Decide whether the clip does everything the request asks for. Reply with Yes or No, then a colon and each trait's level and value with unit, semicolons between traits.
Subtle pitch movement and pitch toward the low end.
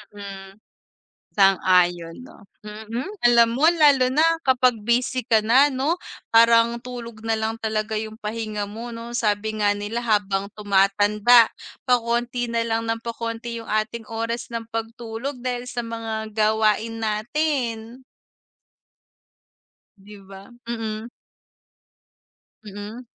No: narrow, 2.1 semitones; high, 225 Hz